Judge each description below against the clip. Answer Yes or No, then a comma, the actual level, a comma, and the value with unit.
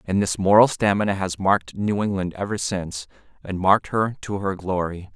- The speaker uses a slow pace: No, average, 185 wpm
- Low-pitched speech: Yes, very low, 95 Hz